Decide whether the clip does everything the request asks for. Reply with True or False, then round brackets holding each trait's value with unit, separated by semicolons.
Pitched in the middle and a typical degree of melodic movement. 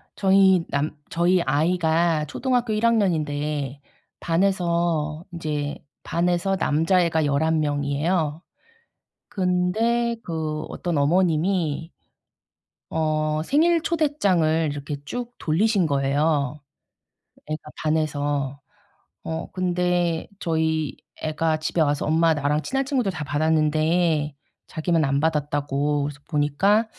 True (160 Hz; 3.3 semitones)